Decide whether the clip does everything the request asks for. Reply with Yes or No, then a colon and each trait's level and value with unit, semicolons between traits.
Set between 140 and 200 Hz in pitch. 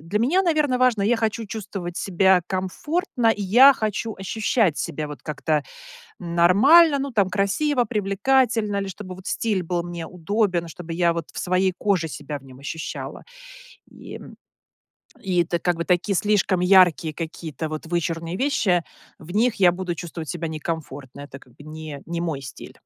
Yes: medium, 185 Hz